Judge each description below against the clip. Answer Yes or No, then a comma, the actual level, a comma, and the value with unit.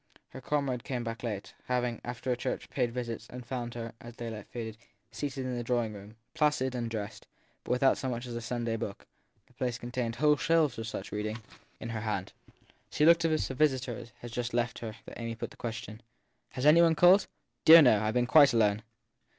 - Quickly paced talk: Yes, fast, 220 wpm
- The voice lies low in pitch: Yes, low, 120 Hz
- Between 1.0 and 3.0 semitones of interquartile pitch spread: Yes, narrow, 2.4 semitones